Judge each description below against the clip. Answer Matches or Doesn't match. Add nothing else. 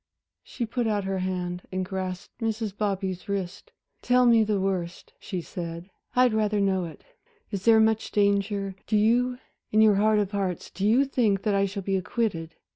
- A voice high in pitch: Matches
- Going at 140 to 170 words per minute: Doesn't match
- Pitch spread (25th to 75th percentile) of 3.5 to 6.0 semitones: Doesn't match